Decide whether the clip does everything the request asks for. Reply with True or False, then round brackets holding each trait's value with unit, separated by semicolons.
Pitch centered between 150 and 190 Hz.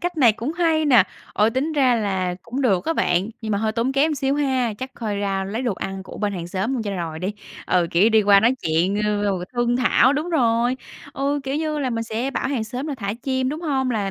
False (235 Hz)